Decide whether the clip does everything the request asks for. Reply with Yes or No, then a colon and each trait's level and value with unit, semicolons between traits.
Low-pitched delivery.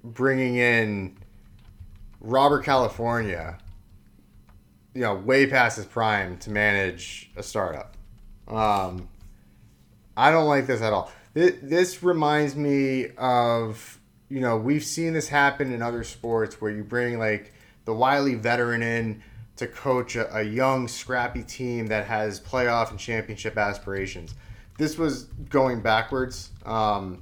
Yes: low, 115 Hz